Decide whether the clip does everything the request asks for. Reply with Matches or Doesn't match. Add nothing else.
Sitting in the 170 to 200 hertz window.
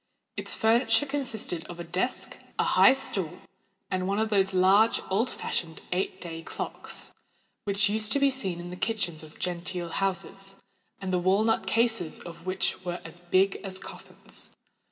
Matches